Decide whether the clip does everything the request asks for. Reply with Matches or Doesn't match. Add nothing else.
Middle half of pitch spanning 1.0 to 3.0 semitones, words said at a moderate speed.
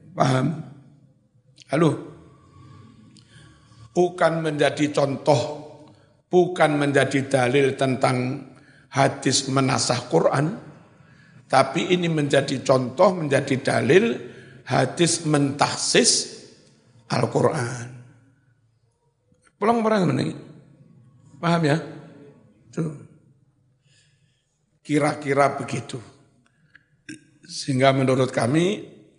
Doesn't match